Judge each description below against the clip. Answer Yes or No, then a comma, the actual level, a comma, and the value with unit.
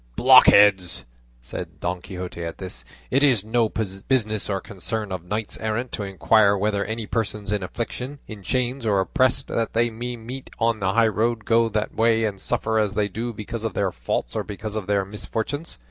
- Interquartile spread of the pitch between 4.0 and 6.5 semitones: No, average, 2.7 semitones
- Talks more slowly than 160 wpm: No, average, 190 wpm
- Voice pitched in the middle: No, low, 110 Hz